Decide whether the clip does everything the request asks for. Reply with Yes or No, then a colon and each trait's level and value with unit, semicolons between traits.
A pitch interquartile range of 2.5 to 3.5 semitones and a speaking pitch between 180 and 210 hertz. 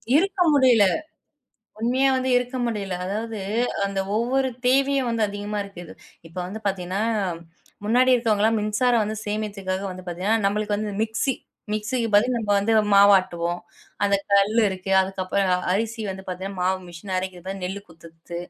Yes: average, 3.2 semitones; high, 205 Hz